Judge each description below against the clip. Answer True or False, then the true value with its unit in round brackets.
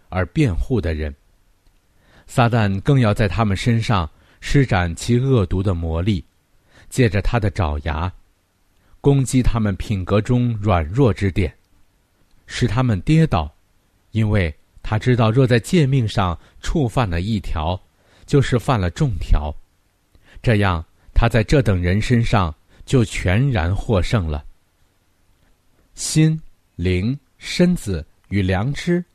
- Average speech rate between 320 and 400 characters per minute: False (180 characters per minute)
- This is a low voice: True (100 Hz)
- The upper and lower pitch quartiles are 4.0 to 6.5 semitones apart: True (5.1 semitones)